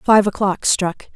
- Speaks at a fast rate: No, average, 155 wpm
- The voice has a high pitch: Yes, high, 200 Hz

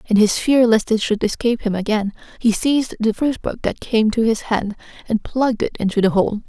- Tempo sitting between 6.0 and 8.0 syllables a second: No, 5.5 syllables/s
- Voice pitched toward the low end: No, high, 225 Hz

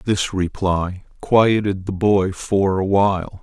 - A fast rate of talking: No, average, 140 wpm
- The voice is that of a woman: No, male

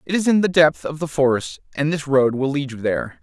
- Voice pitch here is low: No, medium, 145 Hz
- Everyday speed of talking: No, fast, 280 wpm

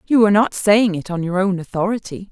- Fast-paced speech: Yes, fast, 235 wpm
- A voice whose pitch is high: Yes, high, 195 Hz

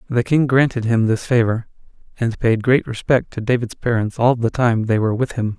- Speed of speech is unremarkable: No, fast, 215 wpm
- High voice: No, low, 120 Hz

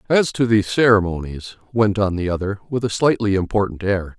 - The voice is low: Yes, low, 100 Hz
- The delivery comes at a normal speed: Yes, average, 185 wpm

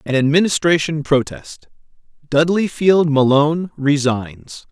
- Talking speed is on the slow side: Yes, slow, 90 wpm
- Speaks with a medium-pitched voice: Yes, medium, 150 Hz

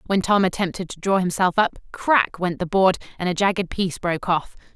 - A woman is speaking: Yes, female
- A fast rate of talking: Yes, fast, 215 wpm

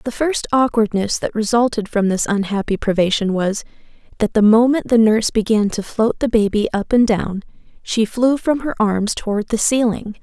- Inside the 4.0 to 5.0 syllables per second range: Yes, 4.9 syllables/s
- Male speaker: No, female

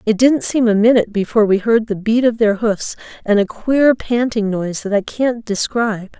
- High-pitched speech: Yes, high, 220 Hz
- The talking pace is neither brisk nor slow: No, fast, 215 wpm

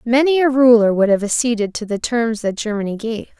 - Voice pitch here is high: Yes, high, 230 Hz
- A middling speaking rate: No, fast, 210 wpm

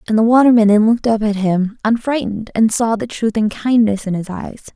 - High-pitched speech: Yes, high, 220 Hz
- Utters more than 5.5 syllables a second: Yes, 5.7 syllables/s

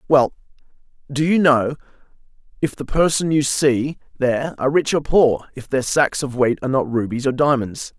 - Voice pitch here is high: No, low, 135 Hz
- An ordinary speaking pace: Yes, average, 180 wpm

